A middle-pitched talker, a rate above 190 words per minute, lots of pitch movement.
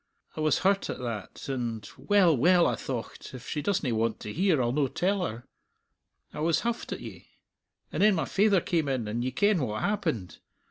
Yes: medium, 150 Hz; average, 200 wpm; wide, 8.0 semitones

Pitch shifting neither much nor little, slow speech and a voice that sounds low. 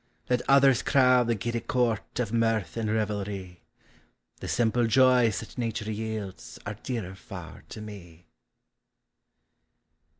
Yes: average, 3.0 semitones; slow, 130 wpm; low, 110 Hz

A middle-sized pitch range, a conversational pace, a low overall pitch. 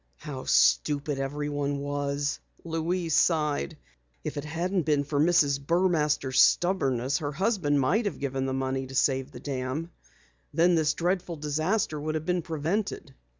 No: average, 3.2 semitones; average, 150 wpm; medium, 150 Hz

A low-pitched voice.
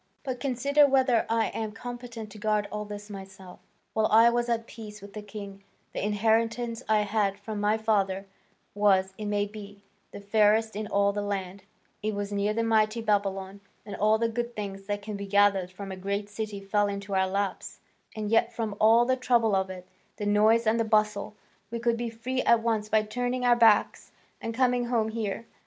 No: high, 215 Hz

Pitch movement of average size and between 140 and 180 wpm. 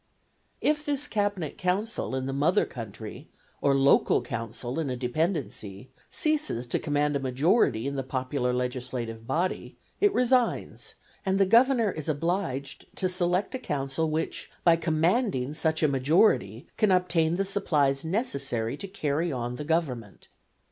No: wide, 6.4 semitones; average, 150 wpm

